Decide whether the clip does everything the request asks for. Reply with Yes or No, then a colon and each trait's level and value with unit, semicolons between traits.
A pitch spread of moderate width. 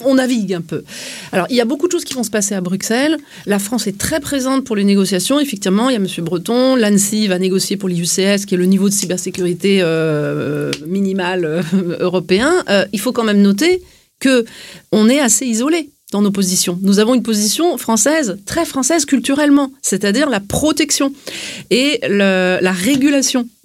No: wide, 6.2 semitones